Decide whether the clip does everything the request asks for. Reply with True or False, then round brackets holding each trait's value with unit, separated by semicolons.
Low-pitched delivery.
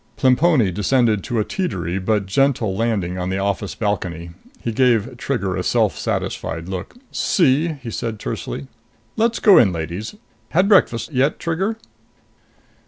True (115 Hz)